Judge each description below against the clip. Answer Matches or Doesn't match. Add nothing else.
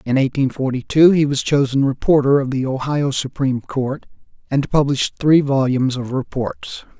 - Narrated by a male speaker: Matches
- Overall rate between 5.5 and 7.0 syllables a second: Doesn't match